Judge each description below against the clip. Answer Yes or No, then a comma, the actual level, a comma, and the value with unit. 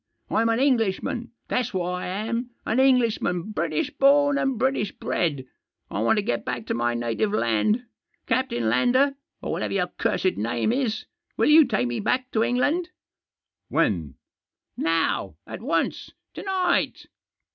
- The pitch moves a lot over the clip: Yes, wide, 8.0 semitones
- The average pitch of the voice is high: Yes, high, 220 Hz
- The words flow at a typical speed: Yes, average, 170 wpm